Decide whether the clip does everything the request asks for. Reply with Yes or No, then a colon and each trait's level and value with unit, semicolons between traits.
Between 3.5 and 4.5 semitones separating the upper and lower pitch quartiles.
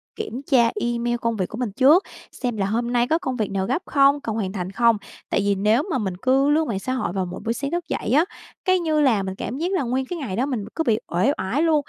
No: average, 5.2 semitones